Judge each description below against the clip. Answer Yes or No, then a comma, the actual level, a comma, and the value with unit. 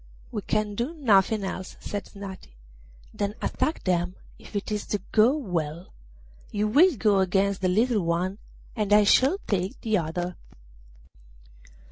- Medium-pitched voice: No, high, 200 Hz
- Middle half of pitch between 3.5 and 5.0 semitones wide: No, average, 2.8 semitones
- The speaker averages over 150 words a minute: No, average, 145 wpm